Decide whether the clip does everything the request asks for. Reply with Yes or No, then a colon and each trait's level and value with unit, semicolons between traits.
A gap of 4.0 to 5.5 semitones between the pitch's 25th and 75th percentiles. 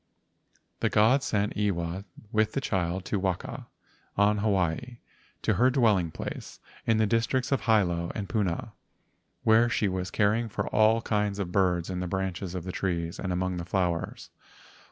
No: average, 3.4 semitones